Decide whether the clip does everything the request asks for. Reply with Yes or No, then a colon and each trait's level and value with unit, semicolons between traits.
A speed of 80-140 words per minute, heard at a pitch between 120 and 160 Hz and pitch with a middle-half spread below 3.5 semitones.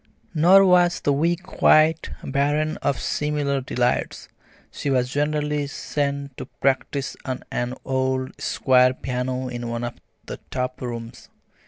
Yes: slow, 135 wpm; medium, 140 Hz; average, 2.8 semitones